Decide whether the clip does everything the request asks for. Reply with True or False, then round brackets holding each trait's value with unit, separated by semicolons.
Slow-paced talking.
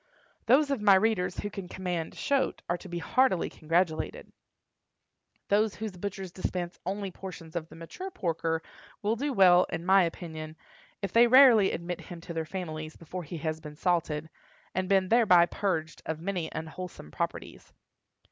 False (165 wpm)